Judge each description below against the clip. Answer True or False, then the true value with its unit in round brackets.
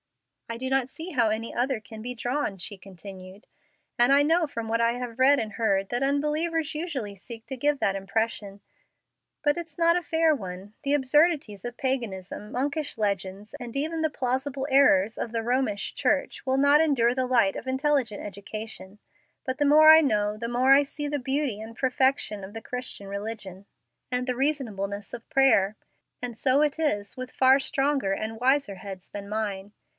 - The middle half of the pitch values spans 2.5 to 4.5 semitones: False (5.2 semitones)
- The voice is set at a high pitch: True (245 Hz)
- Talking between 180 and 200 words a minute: True (185 wpm)